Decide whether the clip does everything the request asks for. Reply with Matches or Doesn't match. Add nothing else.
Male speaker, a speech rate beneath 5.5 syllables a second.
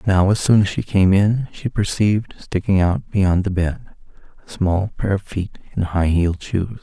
Matches